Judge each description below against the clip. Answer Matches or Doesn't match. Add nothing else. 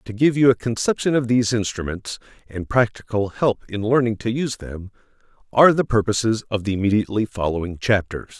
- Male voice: Matches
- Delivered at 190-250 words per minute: Doesn't match